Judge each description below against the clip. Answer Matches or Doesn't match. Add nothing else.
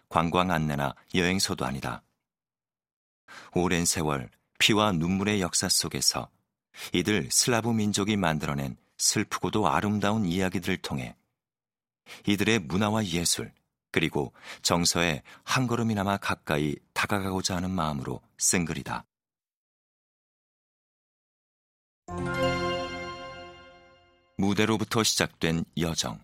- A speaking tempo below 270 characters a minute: Matches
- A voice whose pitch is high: Doesn't match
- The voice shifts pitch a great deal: Doesn't match